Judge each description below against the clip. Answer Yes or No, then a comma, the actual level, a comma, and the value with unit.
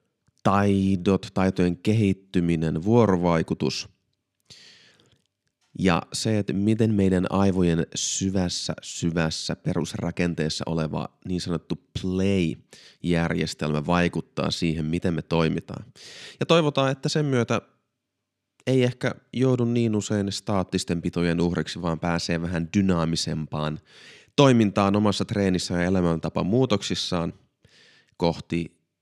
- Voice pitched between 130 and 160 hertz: No, very low, 90 Hz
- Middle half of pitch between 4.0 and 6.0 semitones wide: No, average, 3.5 semitones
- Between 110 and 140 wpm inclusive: No, slow, 95 wpm